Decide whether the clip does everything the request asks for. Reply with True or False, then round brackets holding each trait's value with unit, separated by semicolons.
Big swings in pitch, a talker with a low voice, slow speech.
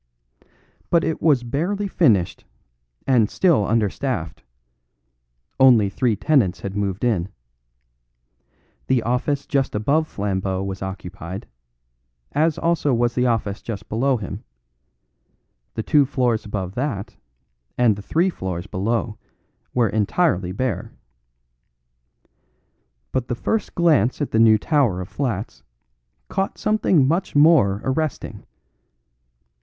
True (6.3 semitones; 120 Hz; 115 wpm)